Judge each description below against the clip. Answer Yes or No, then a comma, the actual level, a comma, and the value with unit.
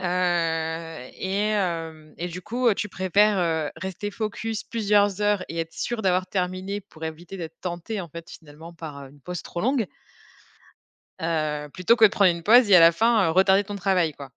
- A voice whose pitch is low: No, medium, 180 Hz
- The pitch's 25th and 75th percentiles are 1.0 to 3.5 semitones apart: No, average, 3.9 semitones